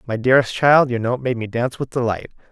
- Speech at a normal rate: No, fast, 215 wpm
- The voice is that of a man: Yes, male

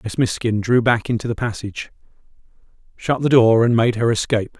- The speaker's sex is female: No, male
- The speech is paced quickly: No, average, 185 wpm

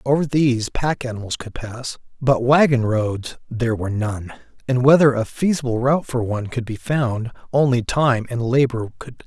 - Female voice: No, male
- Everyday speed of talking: Yes, average, 180 wpm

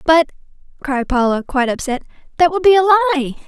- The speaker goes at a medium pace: Yes, average, 175 wpm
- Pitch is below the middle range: No, very high, 305 Hz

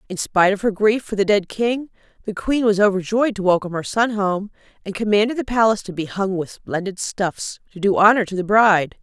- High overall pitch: Yes, high, 205 Hz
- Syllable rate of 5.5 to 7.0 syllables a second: Yes, 5.7 syllables/s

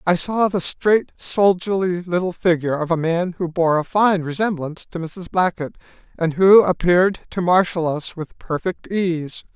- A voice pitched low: No, medium, 175 Hz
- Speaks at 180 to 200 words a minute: No, average, 170 wpm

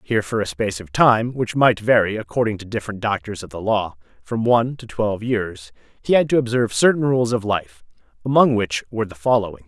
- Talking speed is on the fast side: Yes, fast, 210 wpm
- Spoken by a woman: No, male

